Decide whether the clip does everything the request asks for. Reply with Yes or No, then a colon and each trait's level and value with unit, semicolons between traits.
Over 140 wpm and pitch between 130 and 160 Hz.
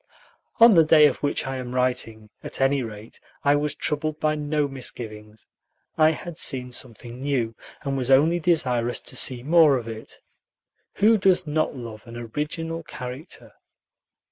Yes: average, 160 wpm; low, 135 Hz